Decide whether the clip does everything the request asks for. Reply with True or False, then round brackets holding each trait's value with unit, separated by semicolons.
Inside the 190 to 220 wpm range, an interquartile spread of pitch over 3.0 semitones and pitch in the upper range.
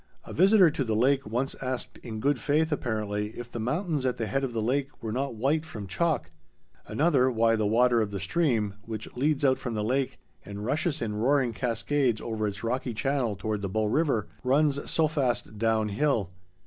False (195 wpm; 4.6 semitones; 120 Hz)